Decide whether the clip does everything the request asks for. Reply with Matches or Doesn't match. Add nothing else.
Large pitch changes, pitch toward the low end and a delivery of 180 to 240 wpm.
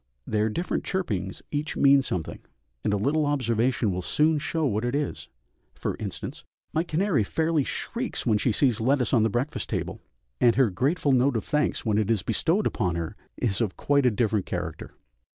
Matches